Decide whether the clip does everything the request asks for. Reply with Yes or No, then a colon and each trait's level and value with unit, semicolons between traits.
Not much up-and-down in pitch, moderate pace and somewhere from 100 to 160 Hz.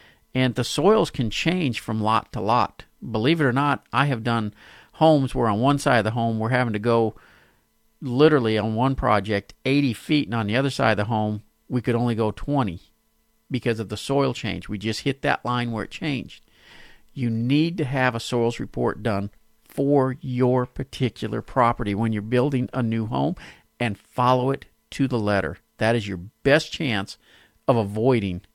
No: average, 3.3 semitones; average, 190 wpm; low, 120 Hz